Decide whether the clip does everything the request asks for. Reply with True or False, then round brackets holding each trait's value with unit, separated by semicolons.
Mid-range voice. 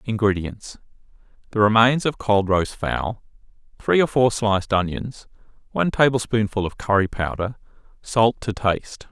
False (110 Hz)